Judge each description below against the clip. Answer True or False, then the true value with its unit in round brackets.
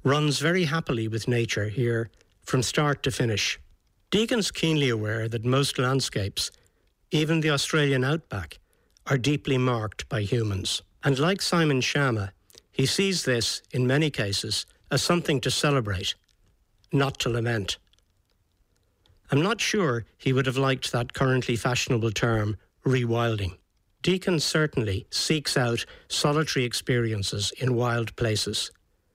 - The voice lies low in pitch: True (125 Hz)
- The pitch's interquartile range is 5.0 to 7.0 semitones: True (5.4 semitones)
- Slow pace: True (130 wpm)